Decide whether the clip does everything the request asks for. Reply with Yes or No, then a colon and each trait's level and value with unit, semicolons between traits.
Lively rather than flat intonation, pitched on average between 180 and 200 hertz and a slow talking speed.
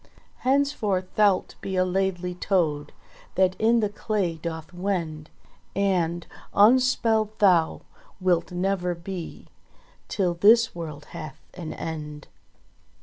No: average, 3.4 semitones; medium, 185 Hz; slow, 110 wpm